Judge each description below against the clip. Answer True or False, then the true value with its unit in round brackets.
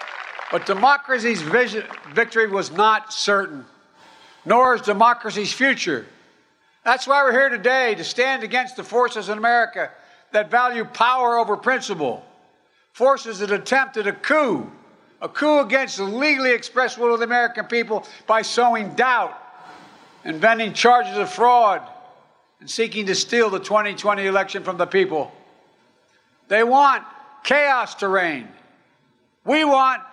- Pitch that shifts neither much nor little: True (3.5 semitones)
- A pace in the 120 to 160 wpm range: True (135 wpm)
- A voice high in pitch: True (235 Hz)